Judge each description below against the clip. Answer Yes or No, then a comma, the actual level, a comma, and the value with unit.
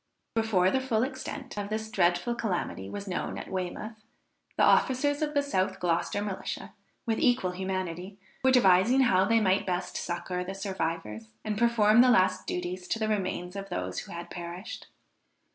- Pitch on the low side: No, high, 195 Hz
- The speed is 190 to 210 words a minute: No, average, 170 wpm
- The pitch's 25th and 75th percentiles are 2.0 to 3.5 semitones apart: No, average, 4.0 semitones